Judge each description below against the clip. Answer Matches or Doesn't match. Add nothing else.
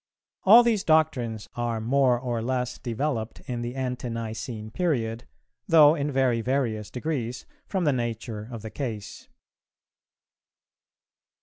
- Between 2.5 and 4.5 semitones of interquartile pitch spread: Matches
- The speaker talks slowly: Matches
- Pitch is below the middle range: Matches